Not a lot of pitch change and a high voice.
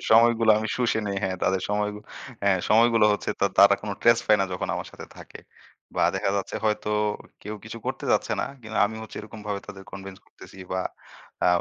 No: narrow, 2.1 semitones; low, 105 Hz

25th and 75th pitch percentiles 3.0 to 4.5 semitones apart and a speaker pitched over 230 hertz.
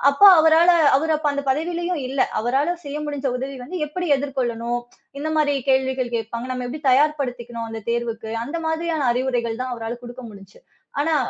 Yes: average, 4.2 semitones; very high, 265 Hz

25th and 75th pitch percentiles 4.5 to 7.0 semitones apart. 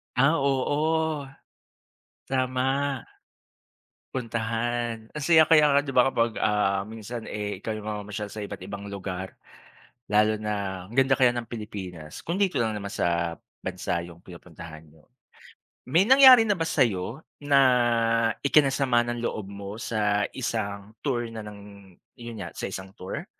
Yes: average, 5.0 semitones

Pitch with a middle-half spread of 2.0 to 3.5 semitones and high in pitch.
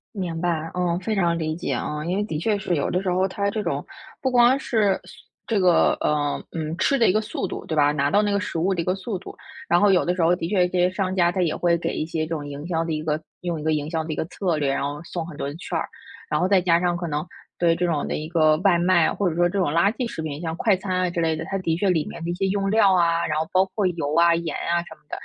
No: average, 3.0 semitones; medium, 175 Hz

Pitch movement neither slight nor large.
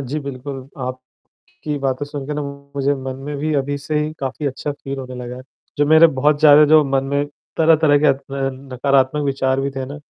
No: narrow, 1.7 semitones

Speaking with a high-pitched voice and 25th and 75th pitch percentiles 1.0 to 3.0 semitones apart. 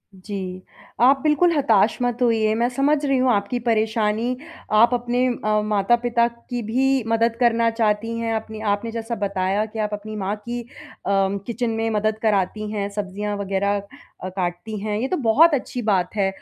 Yes: high, 220 Hz; narrow, 2.6 semitones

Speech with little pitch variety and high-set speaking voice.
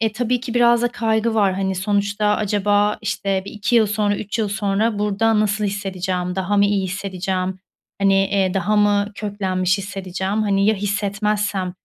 Yes: narrow, 1.5 semitones; high, 205 Hz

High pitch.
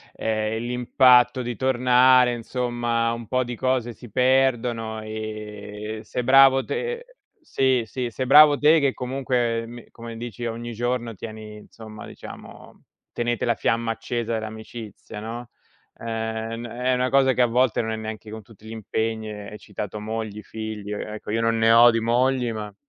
No: low, 115 Hz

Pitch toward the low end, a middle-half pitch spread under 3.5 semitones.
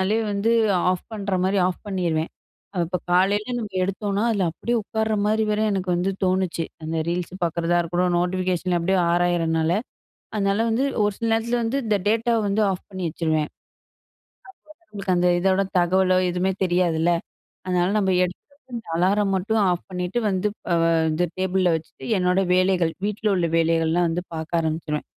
No: medium, 185 Hz; average, 2.8 semitones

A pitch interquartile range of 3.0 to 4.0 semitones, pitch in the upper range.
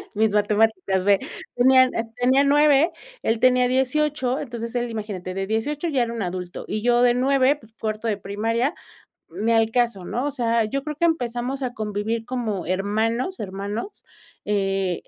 Yes: average, 3.6 semitones; high, 230 Hz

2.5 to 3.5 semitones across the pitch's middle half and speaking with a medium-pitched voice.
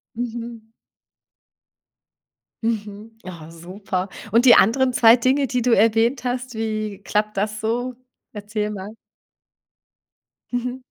No: average, 2.8 semitones; high, 225 Hz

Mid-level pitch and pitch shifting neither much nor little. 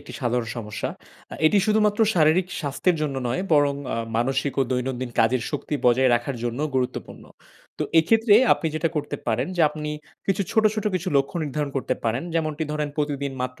Yes: medium, 145 Hz; average, 4.2 semitones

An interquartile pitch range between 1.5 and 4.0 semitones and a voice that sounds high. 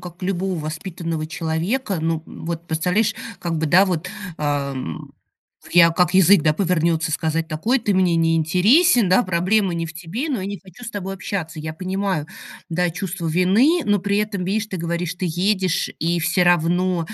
No: average, 2.9 semitones; medium, 180 Hz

